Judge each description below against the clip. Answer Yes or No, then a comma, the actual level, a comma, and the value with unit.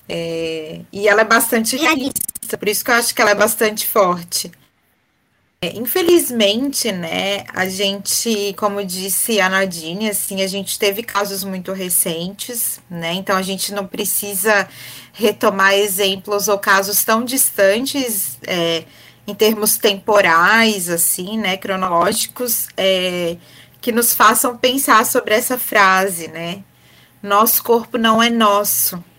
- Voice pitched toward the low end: No, high, 205 Hz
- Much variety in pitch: No, average, 2.9 semitones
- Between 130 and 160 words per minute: Yes, average, 135 wpm